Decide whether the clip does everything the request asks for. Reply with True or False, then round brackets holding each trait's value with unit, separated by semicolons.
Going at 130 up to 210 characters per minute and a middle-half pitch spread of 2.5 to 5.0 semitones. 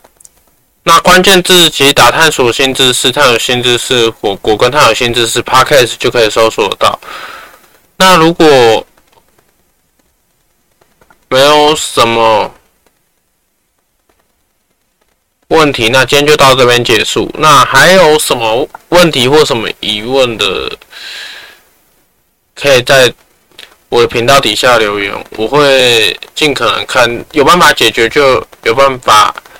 False (190 characters per minute; 6.5 semitones)